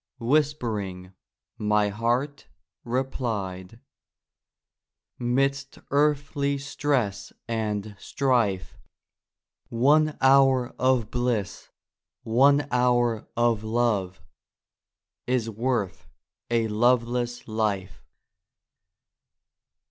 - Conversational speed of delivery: No, slow, 70 wpm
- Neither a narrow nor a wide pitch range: Yes, average, 3.9 semitones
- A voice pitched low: Yes, low, 120 Hz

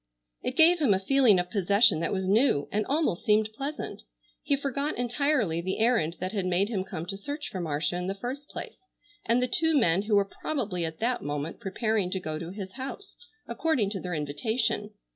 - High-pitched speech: Yes, high, 205 Hz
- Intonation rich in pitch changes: Yes, wide, 5.9 semitones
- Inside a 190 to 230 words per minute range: Yes, fast, 205 wpm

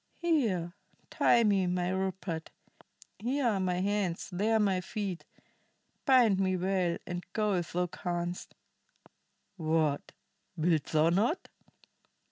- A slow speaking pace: Yes, slow, 115 wpm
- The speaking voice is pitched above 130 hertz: Yes, medium, 185 Hz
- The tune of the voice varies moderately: Yes, average, 3.2 semitones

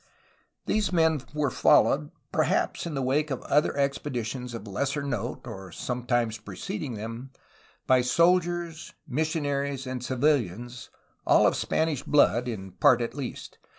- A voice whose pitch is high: No, low, 130 Hz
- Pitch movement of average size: Yes, average, 3.8 semitones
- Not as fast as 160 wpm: Yes, slow, 135 wpm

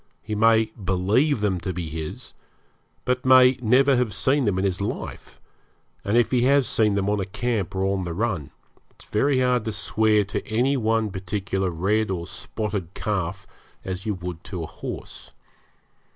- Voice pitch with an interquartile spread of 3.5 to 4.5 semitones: Yes, average, 3.9 semitones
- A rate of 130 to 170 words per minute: No, average, 180 wpm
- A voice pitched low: Yes, low, 105 Hz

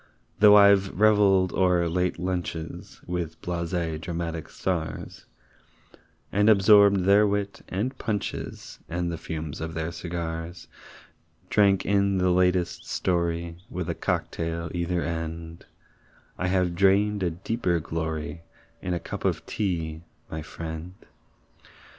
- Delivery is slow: Yes, slow, 125 wpm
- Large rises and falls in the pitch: No, average, 2.8 semitones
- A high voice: No, very low, 90 Hz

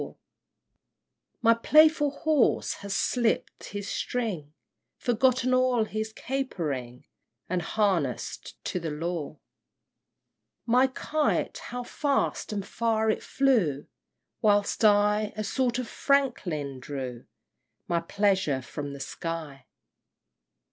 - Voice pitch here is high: Yes, high, 210 Hz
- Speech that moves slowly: Yes, slow, 105 wpm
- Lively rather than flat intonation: Yes, wide, 7.6 semitones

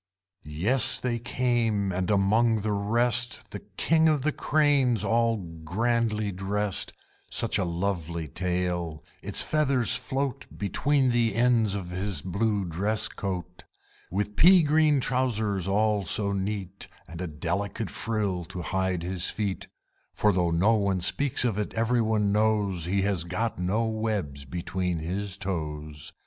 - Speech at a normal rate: Yes, average, 145 wpm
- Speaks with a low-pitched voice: Yes, low, 100 Hz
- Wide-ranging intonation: No, average, 4.1 semitones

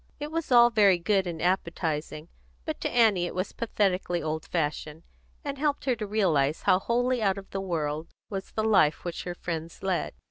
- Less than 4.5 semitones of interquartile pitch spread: No, average, 5.0 semitones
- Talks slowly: No, average, 190 wpm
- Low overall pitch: No, high, 190 Hz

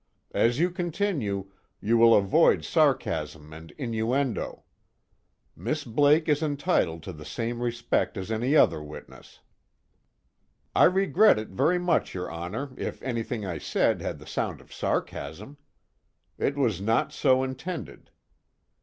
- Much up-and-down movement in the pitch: Yes, wide, 7.0 semitones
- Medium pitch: No, low, 120 Hz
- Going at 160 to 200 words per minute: No, slow, 135 wpm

